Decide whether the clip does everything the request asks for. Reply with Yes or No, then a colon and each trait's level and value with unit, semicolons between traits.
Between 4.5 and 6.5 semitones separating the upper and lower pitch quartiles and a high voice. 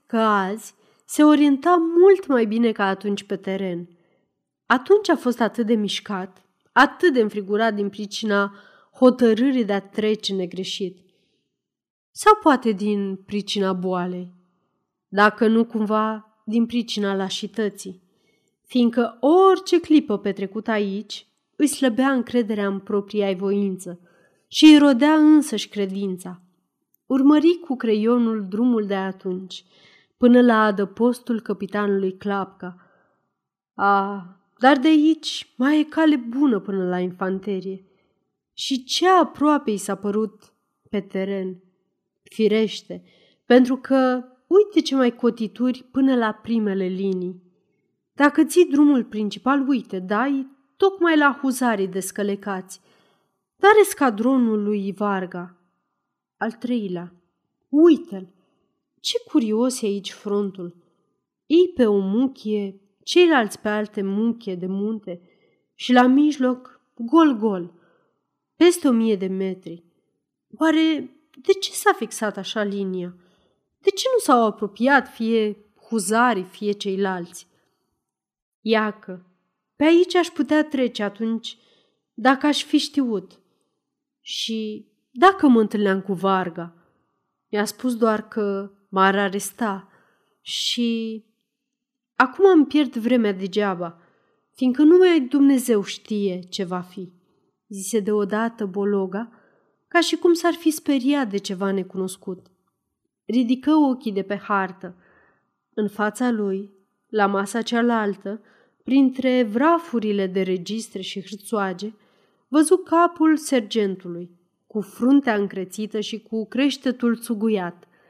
Yes: average, 5.0 semitones; high, 215 Hz